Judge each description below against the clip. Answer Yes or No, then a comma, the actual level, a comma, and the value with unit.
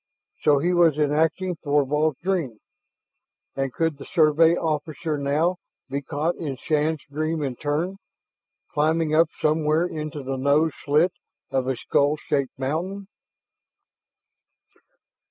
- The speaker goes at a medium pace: No, slow, 120 wpm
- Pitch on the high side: No, medium, 155 Hz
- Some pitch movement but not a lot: No, narrow, 2.3 semitones